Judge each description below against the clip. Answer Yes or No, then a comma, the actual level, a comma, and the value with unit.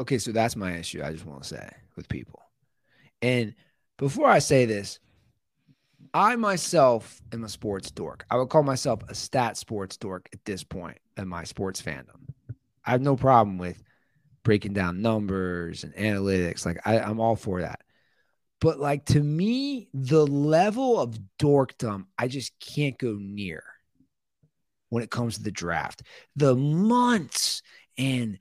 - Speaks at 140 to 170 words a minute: Yes, average, 160 wpm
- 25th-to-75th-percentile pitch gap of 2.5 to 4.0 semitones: No, wide, 5.6 semitones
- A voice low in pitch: Yes, low, 120 Hz